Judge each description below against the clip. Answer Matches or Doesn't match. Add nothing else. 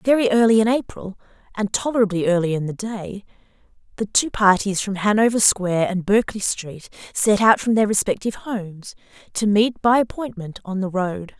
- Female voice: Matches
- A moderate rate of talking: Matches